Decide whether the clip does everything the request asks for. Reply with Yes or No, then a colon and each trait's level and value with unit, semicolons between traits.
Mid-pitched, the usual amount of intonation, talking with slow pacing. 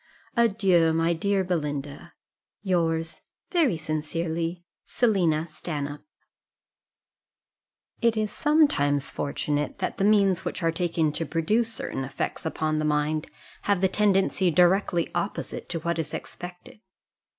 Yes: medium, 170 Hz; average, 3.9 semitones; slow, 120 wpm